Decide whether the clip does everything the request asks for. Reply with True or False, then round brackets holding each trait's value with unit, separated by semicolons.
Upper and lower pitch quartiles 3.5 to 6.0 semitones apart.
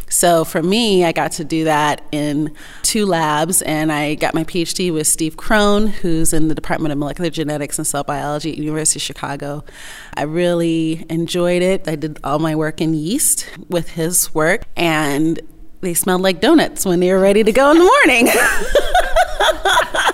False (2.6 semitones)